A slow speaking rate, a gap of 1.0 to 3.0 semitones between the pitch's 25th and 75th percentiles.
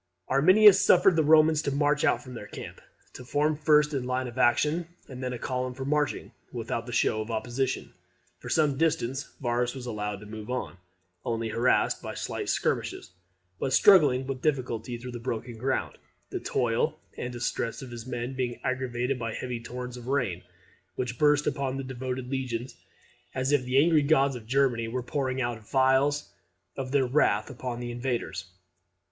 No: average, 185 wpm; average, 2.7 semitones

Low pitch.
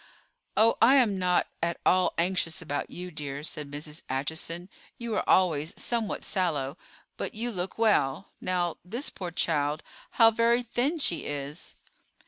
No: medium, 180 Hz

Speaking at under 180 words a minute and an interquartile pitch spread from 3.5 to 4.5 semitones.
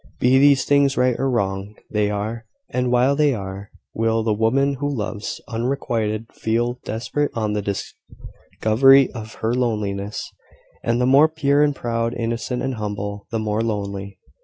Yes: average, 160 wpm; average, 3.8 semitones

